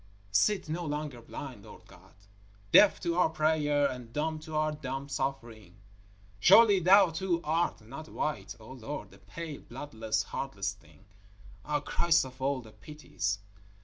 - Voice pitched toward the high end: No, medium, 145 Hz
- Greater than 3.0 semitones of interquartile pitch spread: Yes, average, 5.1 semitones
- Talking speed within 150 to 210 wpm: Yes, average, 155 wpm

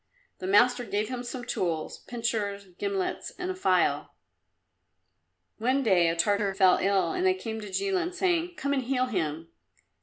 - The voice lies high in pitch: Yes, high, 225 Hz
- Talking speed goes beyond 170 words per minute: No, average, 160 wpm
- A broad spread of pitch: Yes, wide, 6.1 semitones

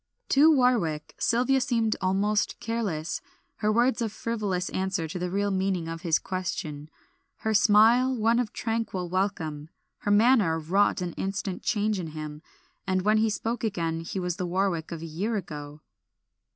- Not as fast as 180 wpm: Yes, average, 165 wpm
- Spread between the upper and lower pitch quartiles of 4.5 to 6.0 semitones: Yes, average, 4.9 semitones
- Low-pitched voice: No, high, 195 Hz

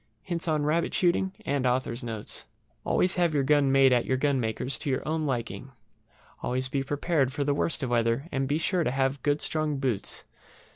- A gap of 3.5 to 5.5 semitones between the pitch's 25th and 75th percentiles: No, average, 2.9 semitones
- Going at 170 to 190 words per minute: Yes, average, 180 wpm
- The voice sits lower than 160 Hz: Yes, medium, 140 Hz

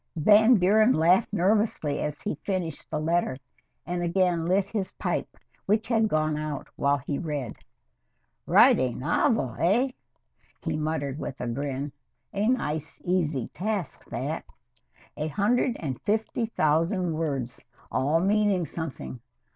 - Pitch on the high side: No, medium, 165 Hz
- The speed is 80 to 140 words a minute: Yes, slow, 135 wpm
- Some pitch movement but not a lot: No, wide, 5.7 semitones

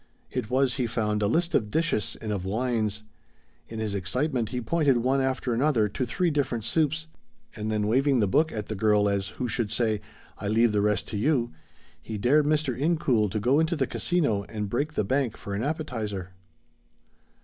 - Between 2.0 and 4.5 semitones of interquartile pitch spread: No, average, 5.0 semitones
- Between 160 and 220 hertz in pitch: No, low, 120 Hz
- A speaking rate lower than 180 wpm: No, average, 195 wpm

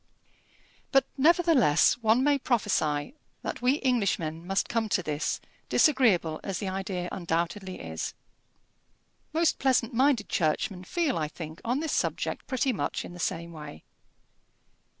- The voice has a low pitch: No, high, 200 Hz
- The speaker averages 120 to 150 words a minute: Yes, slow, 135 wpm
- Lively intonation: Yes, wide, 7.7 semitones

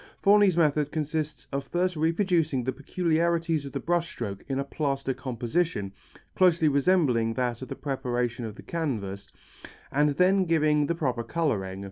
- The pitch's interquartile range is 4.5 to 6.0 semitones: Yes, average, 5.1 semitones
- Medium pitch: Yes, medium, 150 Hz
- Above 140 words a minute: Yes, average, 155 wpm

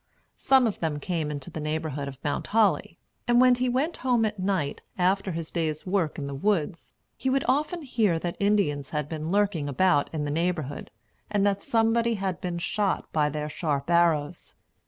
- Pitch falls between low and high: Yes, medium, 175 Hz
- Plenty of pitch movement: Yes, wide, 5.7 semitones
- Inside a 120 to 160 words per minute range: No, average, 190 wpm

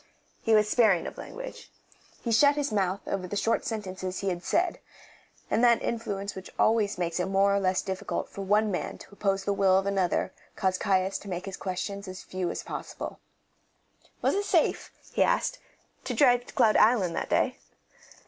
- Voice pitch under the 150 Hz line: No, high, 200 Hz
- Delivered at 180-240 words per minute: Yes, average, 190 wpm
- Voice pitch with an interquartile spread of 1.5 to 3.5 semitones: Yes, average, 3.0 semitones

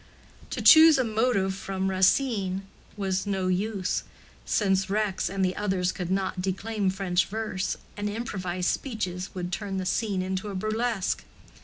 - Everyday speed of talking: Yes, average, 150 wpm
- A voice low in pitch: No, high, 195 Hz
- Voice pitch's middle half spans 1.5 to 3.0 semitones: Yes, narrow, 2.4 semitones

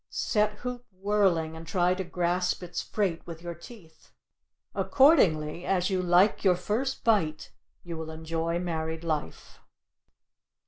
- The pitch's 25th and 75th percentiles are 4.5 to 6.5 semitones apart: No, average, 3.7 semitones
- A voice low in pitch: No, medium, 175 Hz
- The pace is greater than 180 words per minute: No, slow, 135 wpm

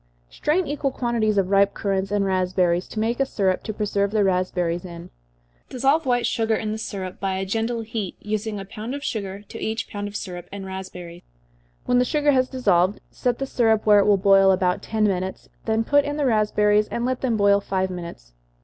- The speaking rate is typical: No, fast, 215 wpm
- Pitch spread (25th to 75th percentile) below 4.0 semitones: Yes, average, 3.4 semitones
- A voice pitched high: Yes, high, 205 Hz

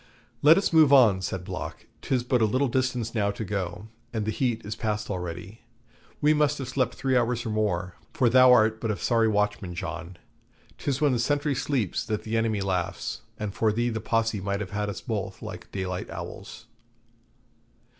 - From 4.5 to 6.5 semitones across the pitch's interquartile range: No, average, 3.8 semitones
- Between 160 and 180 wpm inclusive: No, average, 195 wpm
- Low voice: Yes, low, 110 Hz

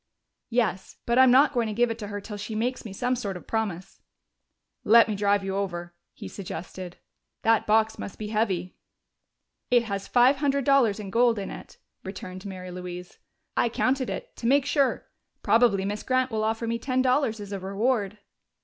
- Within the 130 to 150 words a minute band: No, average, 190 wpm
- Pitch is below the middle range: No, high, 220 Hz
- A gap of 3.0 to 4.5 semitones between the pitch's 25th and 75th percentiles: Yes, average, 3.8 semitones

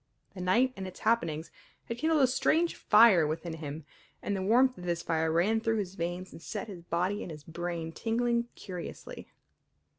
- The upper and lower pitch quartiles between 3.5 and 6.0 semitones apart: Yes, average, 5.3 semitones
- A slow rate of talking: No, average, 185 wpm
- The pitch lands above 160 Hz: Yes, medium, 185 Hz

